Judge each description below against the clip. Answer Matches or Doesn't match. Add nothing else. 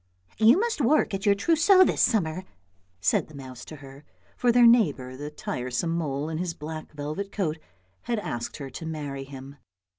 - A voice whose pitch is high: Doesn't match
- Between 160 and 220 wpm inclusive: Matches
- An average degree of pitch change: Doesn't match